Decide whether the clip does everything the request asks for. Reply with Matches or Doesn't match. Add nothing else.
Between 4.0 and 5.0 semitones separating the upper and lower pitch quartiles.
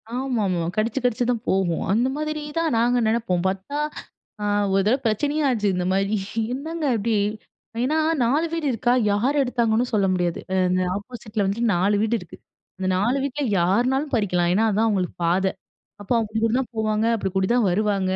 Matches